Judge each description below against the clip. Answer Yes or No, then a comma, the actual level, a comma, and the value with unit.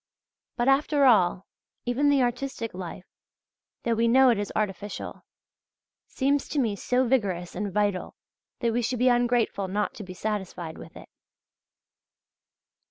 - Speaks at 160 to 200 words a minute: No, average, 145 wpm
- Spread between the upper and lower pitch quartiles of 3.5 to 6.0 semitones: Yes, average, 4.2 semitones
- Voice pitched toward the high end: Yes, high, 230 Hz